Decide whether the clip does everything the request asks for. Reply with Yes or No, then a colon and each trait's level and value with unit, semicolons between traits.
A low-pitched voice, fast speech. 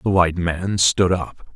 No: very low, 90 Hz; average, 195 wpm